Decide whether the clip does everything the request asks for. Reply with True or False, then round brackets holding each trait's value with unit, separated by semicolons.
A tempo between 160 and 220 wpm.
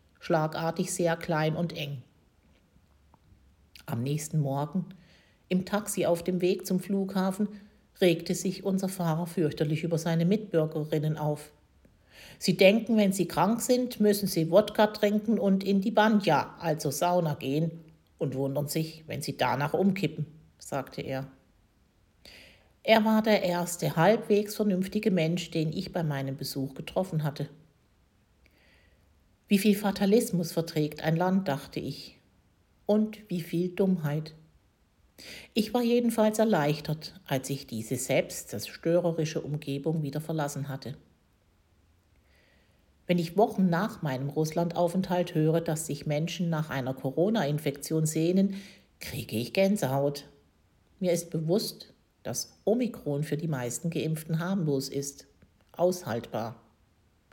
False (125 wpm)